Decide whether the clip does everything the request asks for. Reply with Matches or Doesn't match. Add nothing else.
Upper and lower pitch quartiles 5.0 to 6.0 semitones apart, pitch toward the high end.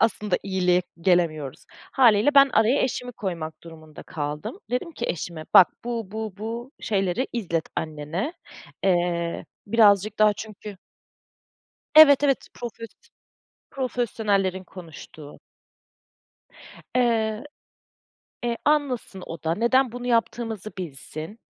Matches